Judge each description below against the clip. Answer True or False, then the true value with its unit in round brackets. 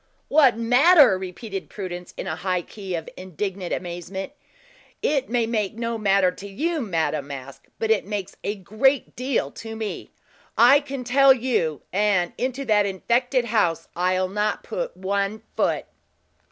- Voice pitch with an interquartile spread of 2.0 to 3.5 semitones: False (4.9 semitones)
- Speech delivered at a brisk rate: False (155 wpm)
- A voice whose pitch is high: True (210 Hz)